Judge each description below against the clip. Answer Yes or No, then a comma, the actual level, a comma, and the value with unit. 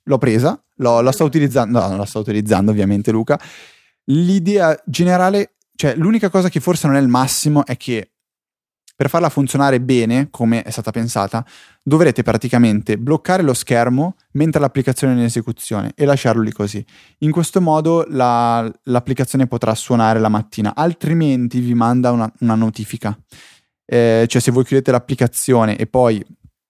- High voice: No, low, 125 Hz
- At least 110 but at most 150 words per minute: No, average, 160 wpm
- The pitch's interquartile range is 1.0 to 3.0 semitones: No, average, 4.4 semitones